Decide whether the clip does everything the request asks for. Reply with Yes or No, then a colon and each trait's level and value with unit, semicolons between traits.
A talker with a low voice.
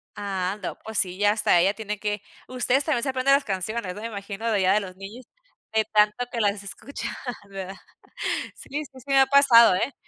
No: high, 210 Hz